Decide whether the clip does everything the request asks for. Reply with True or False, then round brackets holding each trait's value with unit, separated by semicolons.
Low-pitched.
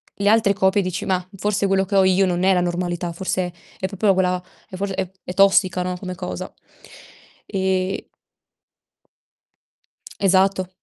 False (190 Hz)